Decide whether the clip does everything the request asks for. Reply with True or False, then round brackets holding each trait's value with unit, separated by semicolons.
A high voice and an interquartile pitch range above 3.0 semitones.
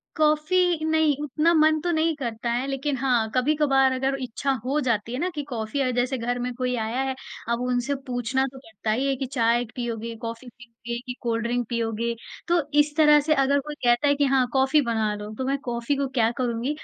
True (255 Hz; 3.4 semitones)